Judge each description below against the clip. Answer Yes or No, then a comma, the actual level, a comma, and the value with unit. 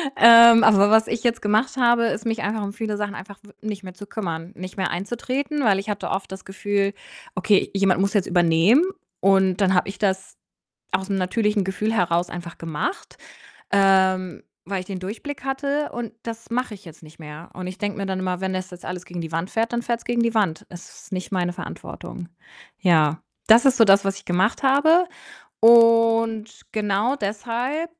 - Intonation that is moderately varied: Yes, average, 3.7 semitones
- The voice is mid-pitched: No, high, 200 Hz